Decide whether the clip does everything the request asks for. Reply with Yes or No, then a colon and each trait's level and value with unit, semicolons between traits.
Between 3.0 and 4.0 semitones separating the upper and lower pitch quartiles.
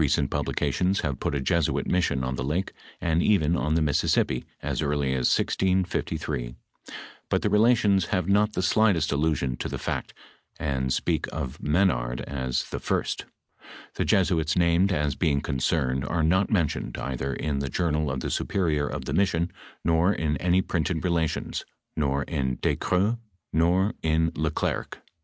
No: average, 4.4 semitones